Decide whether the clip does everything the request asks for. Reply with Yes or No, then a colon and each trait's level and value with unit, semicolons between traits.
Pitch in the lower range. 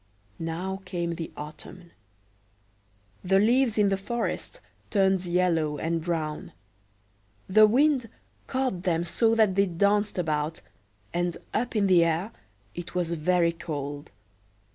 No: medium, 180 Hz